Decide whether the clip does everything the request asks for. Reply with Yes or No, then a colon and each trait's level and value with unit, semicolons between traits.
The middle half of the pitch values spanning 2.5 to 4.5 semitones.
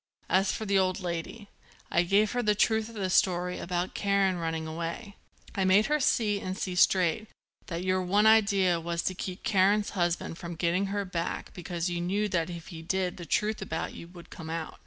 Yes: average, 2.8 semitones